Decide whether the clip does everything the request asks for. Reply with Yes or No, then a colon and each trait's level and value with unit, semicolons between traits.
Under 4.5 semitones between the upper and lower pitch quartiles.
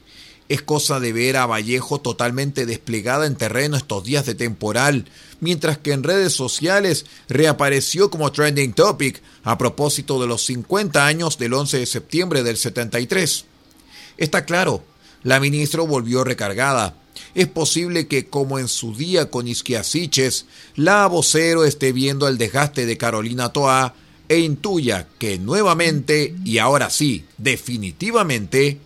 Yes: average, 3.8 semitones